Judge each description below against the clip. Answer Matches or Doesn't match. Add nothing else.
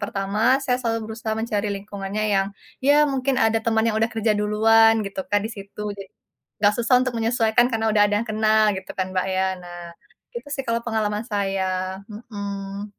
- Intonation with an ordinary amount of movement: Doesn't match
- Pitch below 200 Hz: Doesn't match